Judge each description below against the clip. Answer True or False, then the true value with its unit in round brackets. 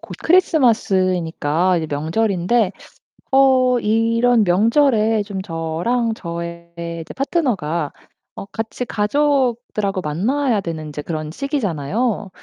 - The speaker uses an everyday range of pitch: False (6.4 semitones)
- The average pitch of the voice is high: True (210 Hz)